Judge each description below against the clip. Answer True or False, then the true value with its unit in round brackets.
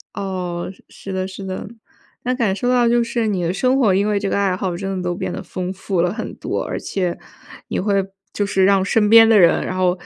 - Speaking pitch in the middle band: False (195 Hz)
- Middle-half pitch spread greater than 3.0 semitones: False (2.7 semitones)